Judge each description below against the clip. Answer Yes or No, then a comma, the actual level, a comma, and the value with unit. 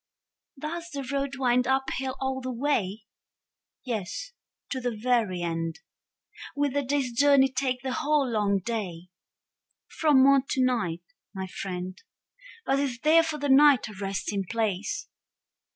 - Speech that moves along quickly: No, average, 145 wpm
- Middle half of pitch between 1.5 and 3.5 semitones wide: No, average, 5.1 semitones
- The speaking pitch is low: No, very high, 255 Hz